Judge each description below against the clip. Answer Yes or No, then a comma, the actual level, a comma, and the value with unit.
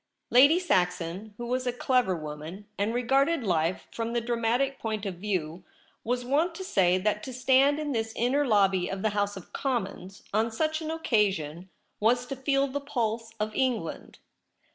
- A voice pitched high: Yes, high, 225 Hz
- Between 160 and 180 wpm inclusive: Yes, average, 175 wpm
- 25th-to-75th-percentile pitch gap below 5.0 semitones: No, average, 5.3 semitones